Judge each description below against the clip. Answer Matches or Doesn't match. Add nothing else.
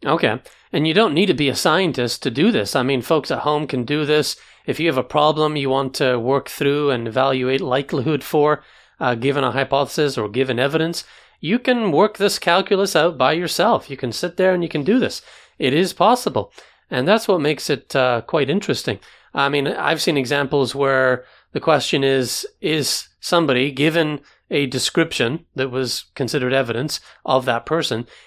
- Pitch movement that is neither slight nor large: Matches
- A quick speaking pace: Doesn't match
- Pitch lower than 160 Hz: Matches